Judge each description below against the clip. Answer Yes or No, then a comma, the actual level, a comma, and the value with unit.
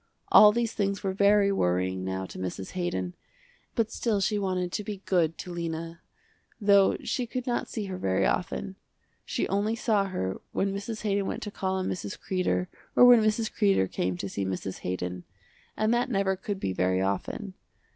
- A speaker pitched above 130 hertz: Yes, high, 190 Hz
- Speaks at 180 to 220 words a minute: Yes, average, 185 wpm